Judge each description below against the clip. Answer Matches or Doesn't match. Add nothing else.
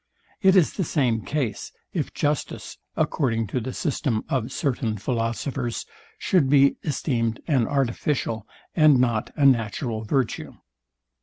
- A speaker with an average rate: Doesn't match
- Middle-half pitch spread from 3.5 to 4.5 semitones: Matches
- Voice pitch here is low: Matches